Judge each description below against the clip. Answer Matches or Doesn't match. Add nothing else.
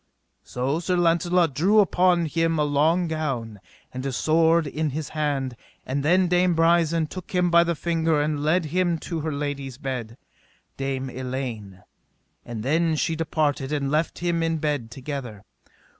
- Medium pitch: Matches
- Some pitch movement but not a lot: Matches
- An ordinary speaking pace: Matches